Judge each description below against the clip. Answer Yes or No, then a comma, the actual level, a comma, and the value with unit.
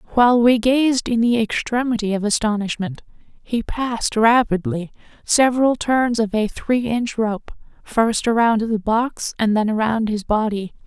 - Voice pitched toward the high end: Yes, high, 225 Hz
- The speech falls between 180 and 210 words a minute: No, average, 150 wpm